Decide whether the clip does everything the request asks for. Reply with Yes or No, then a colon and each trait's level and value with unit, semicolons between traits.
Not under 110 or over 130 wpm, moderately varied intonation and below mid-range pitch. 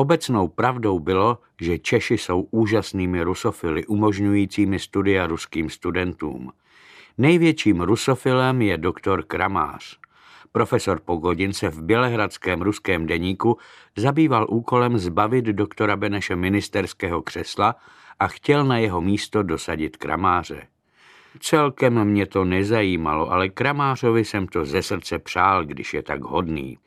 Yes: average, 120 wpm; average, 4.3 semitones; low, 105 Hz